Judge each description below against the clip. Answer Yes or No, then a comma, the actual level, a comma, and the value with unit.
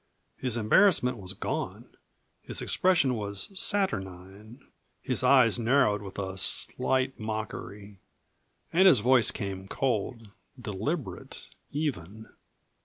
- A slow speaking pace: Yes, slow, 105 wpm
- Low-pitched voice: Yes, low, 110 Hz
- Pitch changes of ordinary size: Yes, average, 4.8 semitones